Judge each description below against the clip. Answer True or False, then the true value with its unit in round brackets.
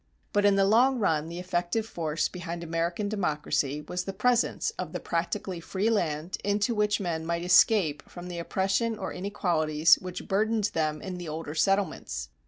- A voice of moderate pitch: True (180 Hz)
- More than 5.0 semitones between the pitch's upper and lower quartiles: False (3.8 semitones)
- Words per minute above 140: True (170 wpm)